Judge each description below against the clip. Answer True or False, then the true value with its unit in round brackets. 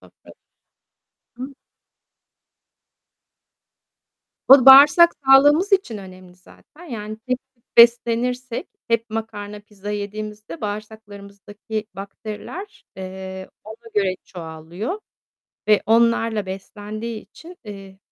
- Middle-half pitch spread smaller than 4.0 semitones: True (2.9 semitones)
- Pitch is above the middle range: True (215 Hz)